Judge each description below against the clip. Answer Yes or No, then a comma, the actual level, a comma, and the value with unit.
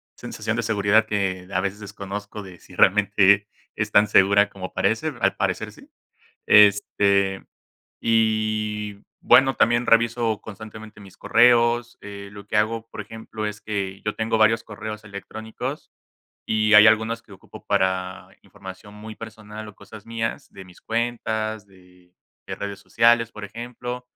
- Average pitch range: No, narrow, 1.9 semitones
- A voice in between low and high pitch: No, low, 105 Hz